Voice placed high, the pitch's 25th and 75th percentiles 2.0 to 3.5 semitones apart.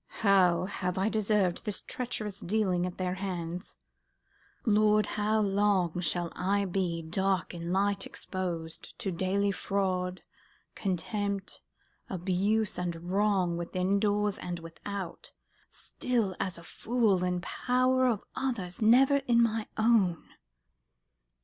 Yes: high, 195 Hz; average, 2.8 semitones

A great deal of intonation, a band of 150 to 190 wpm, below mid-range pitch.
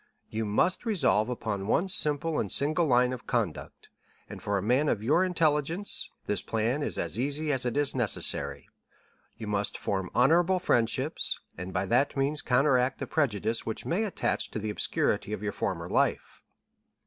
Yes: wide, 5.9 semitones; average, 170 wpm; low, 125 Hz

